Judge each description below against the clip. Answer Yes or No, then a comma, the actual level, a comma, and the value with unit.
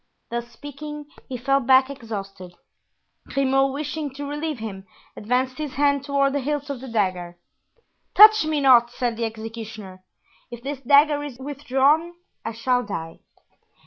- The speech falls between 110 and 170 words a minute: Yes, average, 145 wpm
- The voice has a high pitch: Yes, very high, 265 Hz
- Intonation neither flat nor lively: Yes, average, 4.1 semitones